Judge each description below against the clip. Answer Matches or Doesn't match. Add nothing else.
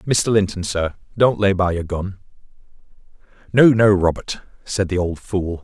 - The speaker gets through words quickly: Doesn't match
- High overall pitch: Doesn't match